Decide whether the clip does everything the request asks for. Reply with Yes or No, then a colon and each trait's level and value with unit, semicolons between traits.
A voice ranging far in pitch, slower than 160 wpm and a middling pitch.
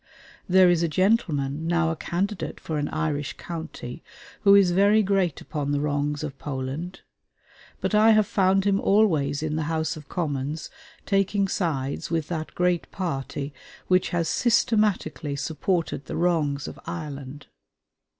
No: average, 4.4 semitones; average, 150 wpm; medium, 165 Hz